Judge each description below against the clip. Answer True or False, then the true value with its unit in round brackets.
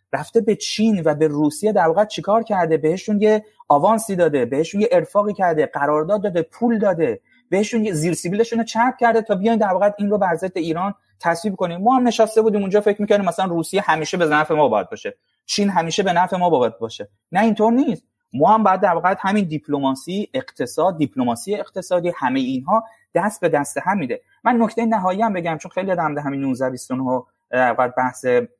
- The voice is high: True (195 Hz)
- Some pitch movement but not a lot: False (5.7 semitones)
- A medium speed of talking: False (195 wpm)